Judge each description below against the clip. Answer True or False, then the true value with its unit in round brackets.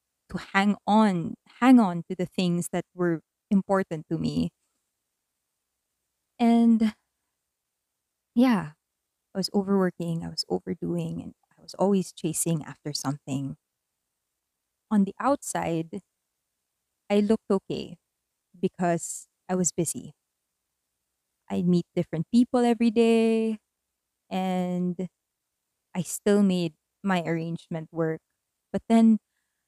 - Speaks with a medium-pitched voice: True (170 Hz)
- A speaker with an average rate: False (105 wpm)